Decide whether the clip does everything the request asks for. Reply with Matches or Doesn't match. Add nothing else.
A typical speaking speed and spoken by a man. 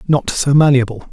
Matches